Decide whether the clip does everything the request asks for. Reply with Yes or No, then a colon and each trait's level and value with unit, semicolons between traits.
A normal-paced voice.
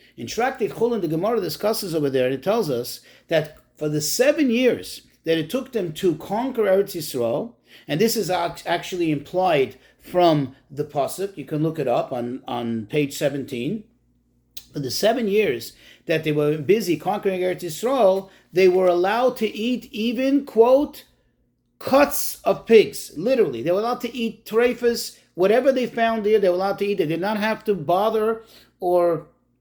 Yes: average, 175 wpm